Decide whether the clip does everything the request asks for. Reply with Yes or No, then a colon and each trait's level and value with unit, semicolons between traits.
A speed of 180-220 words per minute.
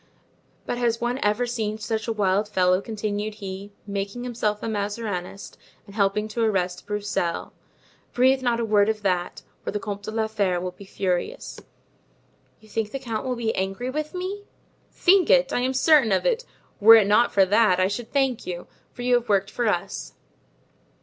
Yes: average, 185 wpm